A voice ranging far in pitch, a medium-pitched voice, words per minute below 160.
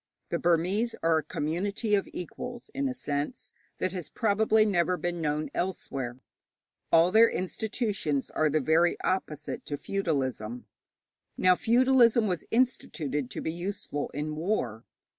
Yes: wide, 6.0 semitones; medium, 175 Hz; average, 140 wpm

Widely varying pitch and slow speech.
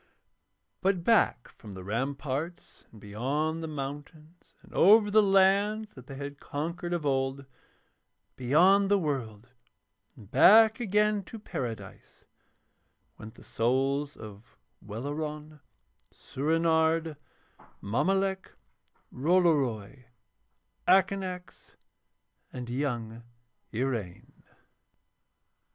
Yes: wide, 6.6 semitones; slow, 90 wpm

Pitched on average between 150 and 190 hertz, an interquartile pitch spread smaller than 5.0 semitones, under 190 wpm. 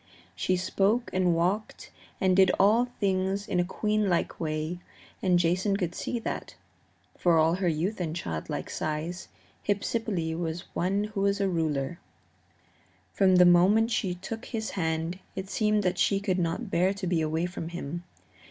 Yes: medium, 185 Hz; average, 3.0 semitones; average, 160 wpm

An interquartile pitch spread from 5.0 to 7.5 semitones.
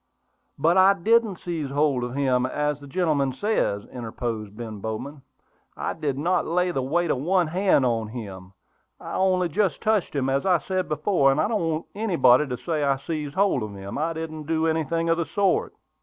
Yes: average, 5.3 semitones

